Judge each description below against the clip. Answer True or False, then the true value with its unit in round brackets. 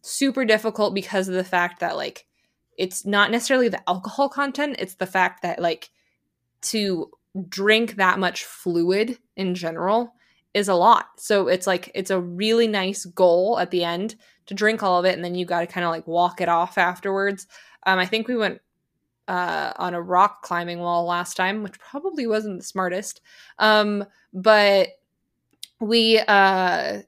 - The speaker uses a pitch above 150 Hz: True (190 Hz)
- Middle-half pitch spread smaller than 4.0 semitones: True (3.3 semitones)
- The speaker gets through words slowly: False (175 wpm)